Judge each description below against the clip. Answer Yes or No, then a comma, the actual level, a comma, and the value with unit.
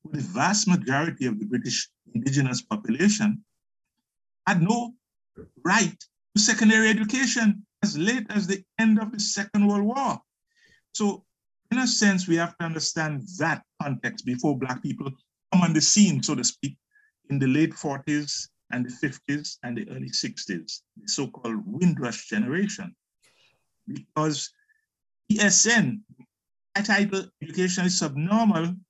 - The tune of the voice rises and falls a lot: Yes, wide, 5.9 semitones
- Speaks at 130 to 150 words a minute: Yes, slow, 135 wpm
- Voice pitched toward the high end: Yes, high, 195 Hz